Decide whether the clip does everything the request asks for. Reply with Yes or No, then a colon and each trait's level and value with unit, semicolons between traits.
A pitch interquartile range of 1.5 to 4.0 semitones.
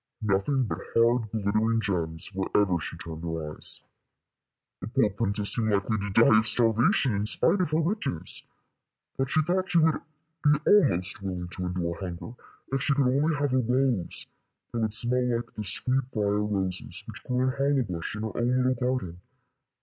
No: average, 4.9 semitones